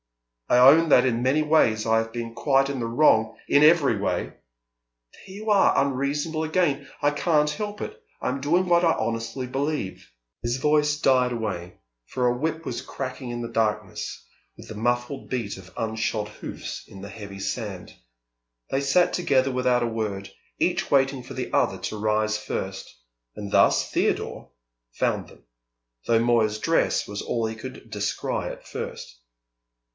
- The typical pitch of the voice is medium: No, low, 125 Hz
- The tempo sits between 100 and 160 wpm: No, average, 170 wpm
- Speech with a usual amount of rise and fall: Yes, average, 4.8 semitones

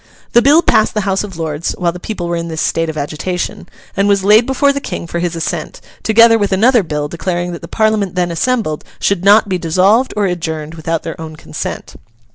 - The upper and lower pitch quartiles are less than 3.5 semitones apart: No, average, 4.5 semitones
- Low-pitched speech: No, medium, 180 Hz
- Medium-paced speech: No, fast, 220 wpm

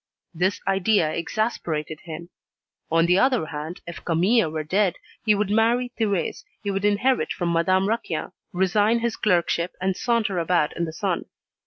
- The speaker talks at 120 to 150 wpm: No, average, 160 wpm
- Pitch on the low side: No, medium, 185 Hz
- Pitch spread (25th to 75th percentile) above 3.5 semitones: Yes, average, 4.2 semitones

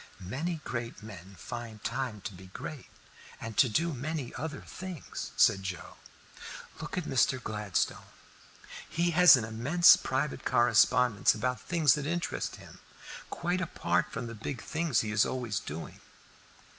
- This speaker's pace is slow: No, average, 145 wpm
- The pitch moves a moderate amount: No, wide, 6.5 semitones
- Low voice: Yes, low, 125 Hz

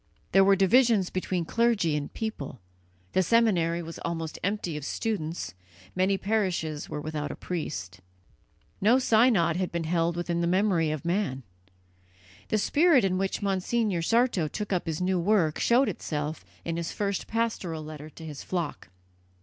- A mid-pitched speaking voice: Yes, medium, 180 Hz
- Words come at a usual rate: Yes, average, 160 wpm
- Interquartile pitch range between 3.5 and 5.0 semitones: Yes, average, 4.5 semitones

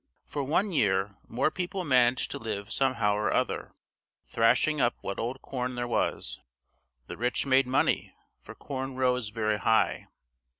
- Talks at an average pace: Yes, average, 155 wpm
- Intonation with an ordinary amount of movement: Yes, average, 3.2 semitones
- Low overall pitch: Yes, low, 125 Hz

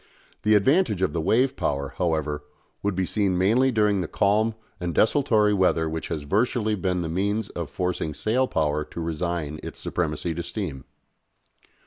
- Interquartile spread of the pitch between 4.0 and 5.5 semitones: Yes, average, 4.7 semitones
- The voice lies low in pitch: Yes, very low, 90 Hz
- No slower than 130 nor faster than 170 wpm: Yes, average, 165 wpm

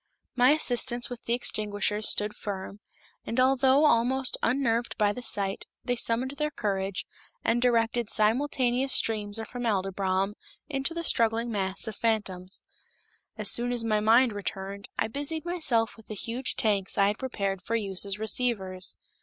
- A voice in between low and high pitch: No, high, 225 Hz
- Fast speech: No, average, 155 wpm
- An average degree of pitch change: Yes, average, 3.5 semitones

